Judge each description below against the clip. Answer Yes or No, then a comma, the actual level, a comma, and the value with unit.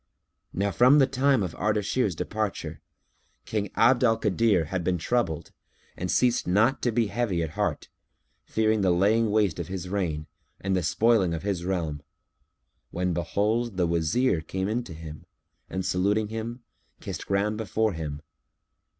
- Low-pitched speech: Yes, low, 100 Hz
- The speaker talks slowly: No, average, 160 wpm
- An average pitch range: Yes, average, 4.4 semitones